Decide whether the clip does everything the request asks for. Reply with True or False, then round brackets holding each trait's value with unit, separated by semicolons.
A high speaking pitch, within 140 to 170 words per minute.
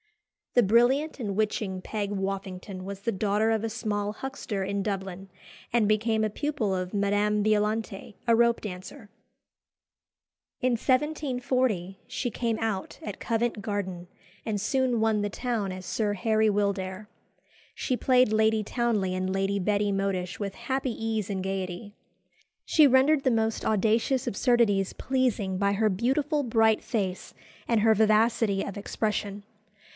True (215 Hz; 145 wpm)